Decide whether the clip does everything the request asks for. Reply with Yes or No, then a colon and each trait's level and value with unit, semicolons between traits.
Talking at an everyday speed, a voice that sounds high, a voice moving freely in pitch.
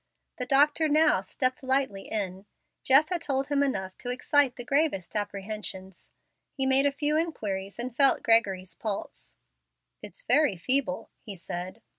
Yes: average, 150 wpm; very high, 250 Hz; wide, 6.3 semitones